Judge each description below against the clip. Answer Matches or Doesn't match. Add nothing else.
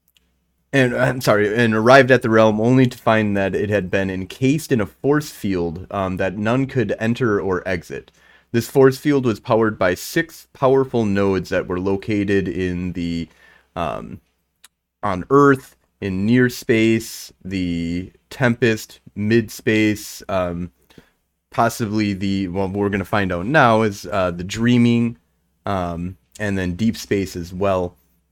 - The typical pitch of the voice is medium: Doesn't match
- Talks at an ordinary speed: Matches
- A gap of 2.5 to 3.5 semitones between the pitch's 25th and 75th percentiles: Doesn't match